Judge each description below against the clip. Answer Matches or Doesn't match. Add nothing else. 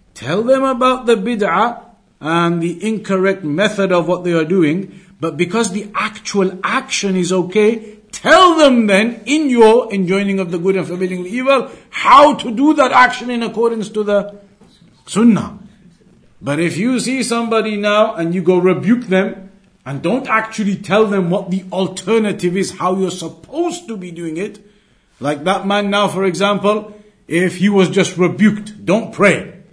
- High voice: Matches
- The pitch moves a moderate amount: Matches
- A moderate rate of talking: Matches